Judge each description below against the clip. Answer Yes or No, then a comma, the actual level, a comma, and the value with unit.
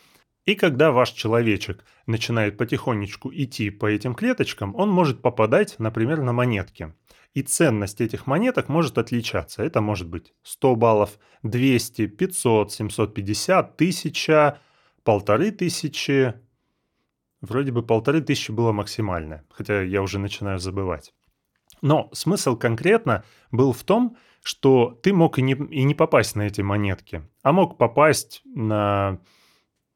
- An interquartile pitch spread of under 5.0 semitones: No, average, 5.3 semitones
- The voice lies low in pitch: Yes, low, 120 Hz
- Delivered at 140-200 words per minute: No, average, 125 wpm